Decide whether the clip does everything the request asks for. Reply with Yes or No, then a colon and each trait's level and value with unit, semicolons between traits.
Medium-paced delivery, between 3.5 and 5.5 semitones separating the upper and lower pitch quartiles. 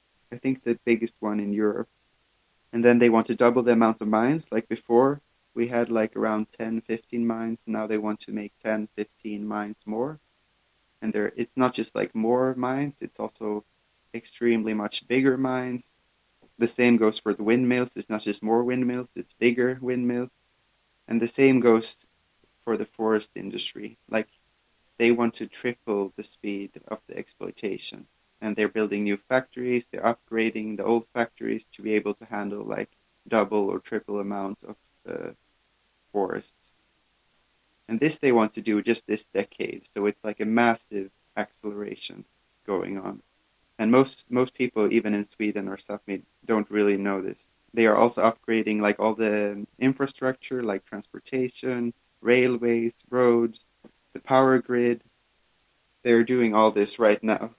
No: average, 155 wpm; narrow, 2.5 semitones